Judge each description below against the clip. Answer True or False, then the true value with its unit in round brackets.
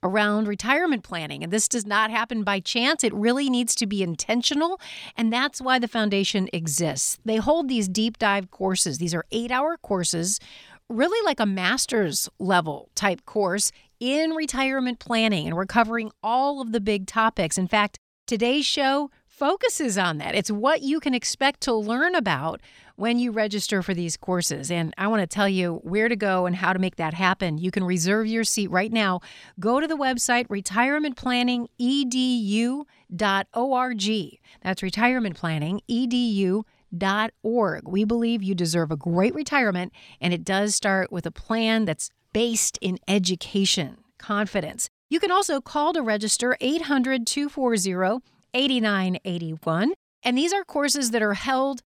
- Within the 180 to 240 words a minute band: False (155 wpm)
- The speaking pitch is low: False (220 Hz)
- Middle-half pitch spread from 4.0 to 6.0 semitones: True (4.9 semitones)